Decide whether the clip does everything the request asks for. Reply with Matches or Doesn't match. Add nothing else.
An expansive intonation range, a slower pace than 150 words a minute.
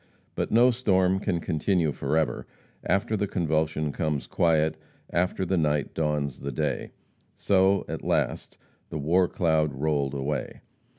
Doesn't match